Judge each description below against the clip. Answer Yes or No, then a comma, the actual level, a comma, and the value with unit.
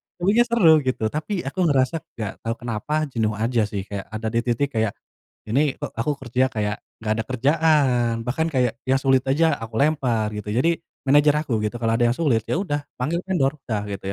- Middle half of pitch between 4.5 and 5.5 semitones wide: Yes, average, 4.9 semitones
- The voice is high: No, low, 125 Hz